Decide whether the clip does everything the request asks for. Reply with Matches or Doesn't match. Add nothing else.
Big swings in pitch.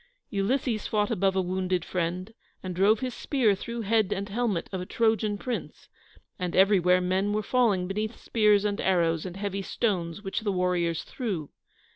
Doesn't match